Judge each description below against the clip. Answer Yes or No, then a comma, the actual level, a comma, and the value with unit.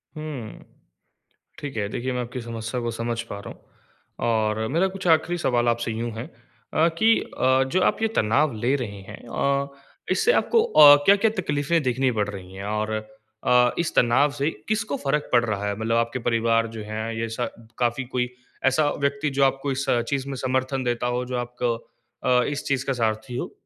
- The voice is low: Yes, low, 125 Hz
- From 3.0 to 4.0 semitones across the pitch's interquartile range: Yes, average, 3.6 semitones